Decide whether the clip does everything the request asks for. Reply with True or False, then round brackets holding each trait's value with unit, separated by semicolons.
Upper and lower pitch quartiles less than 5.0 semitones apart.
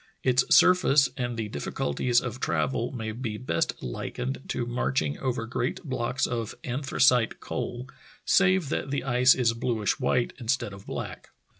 True (2.5 semitones)